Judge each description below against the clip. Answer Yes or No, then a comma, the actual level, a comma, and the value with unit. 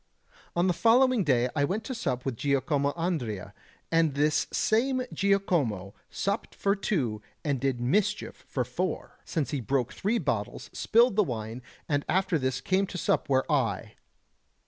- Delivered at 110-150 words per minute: No, average, 160 wpm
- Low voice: No, medium, 150 Hz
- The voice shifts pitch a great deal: Yes, wide, 7.6 semitones